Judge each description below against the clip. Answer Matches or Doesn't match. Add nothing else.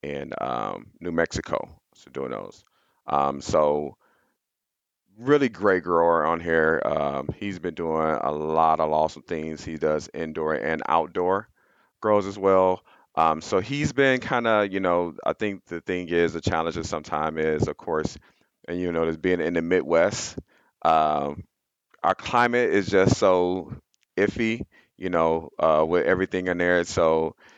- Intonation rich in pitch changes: Doesn't match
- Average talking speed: Matches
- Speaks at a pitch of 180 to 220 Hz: Doesn't match